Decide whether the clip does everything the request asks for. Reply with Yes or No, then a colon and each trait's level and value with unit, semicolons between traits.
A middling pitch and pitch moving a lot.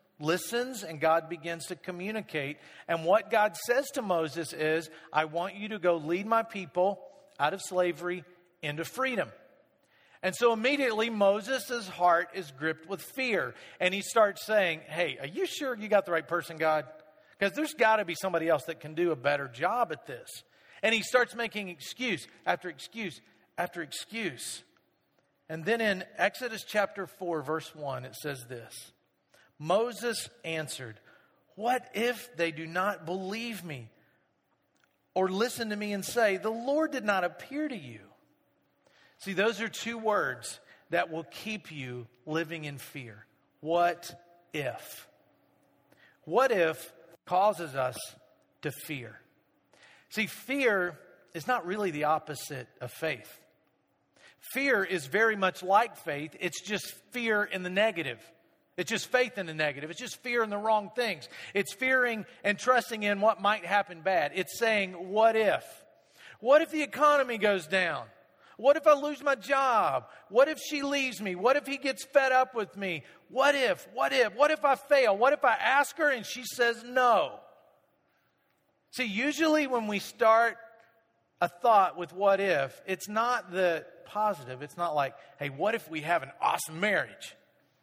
No: high, 195 Hz; wide, 6.0 semitones